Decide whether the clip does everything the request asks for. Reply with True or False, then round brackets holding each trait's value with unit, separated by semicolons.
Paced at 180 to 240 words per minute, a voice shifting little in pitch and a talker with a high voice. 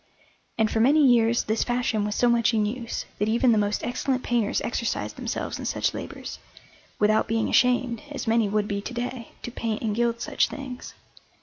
True (195 wpm; 2.1 semitones; 230 Hz)